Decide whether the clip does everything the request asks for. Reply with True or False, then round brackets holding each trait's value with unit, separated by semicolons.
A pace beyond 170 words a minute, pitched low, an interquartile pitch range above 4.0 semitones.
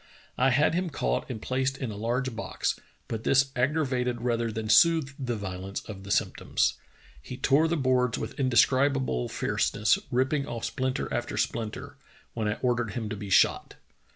False (180 wpm; 125 Hz; 3.4 semitones)